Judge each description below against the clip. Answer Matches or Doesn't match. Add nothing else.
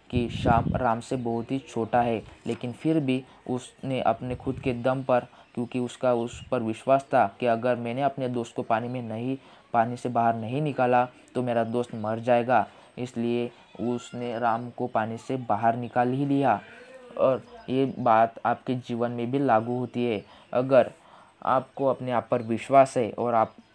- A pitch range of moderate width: Doesn't match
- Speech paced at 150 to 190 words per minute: Matches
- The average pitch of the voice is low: Matches